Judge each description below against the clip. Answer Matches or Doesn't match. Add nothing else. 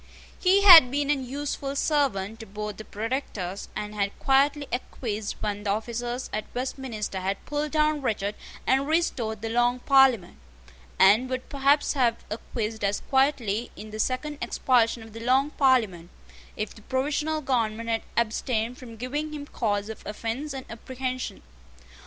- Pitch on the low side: Doesn't match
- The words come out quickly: Doesn't match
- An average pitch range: Matches